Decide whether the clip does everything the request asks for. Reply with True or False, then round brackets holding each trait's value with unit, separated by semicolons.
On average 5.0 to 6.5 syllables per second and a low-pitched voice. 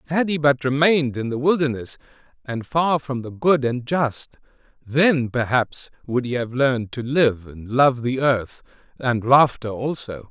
False (4.3 syllables/s; 130 Hz)